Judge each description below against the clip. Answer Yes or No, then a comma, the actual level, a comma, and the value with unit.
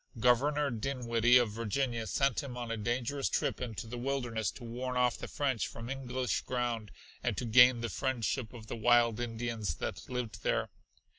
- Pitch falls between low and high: No, low, 120 Hz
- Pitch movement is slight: Yes, narrow, 1.8 semitones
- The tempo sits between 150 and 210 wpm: Yes, average, 175 wpm